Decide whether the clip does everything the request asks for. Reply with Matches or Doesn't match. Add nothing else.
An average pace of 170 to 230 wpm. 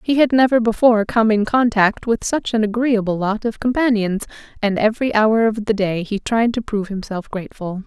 Matches